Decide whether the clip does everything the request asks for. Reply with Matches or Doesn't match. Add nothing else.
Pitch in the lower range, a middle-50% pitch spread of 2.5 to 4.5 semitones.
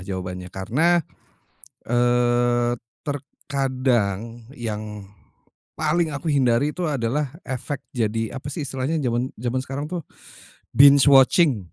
Matches